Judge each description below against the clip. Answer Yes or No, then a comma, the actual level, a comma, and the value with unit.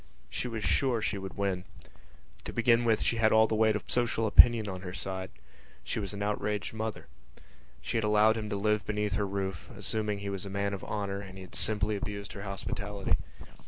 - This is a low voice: Yes, low, 105 Hz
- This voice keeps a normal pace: No, fast, 215 wpm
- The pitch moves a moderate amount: No, narrow, 1.9 semitones